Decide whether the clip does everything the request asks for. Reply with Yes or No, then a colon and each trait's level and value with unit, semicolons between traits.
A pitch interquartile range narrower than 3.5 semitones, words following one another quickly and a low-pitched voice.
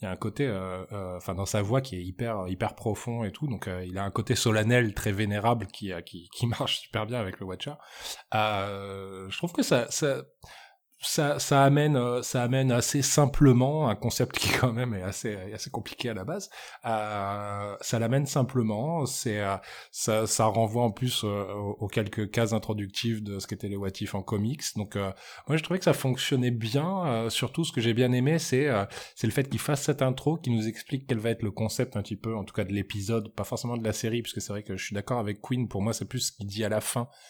No: average, 3.8 semitones; fast, 240 wpm; low, 115 Hz